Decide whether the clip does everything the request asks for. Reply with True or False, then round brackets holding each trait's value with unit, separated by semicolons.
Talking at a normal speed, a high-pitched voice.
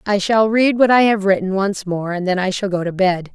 False (285 wpm; 195 Hz)